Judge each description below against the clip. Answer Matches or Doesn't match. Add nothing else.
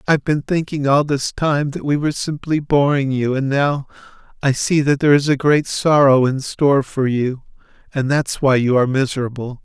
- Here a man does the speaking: Matches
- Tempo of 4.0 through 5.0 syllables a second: Doesn't match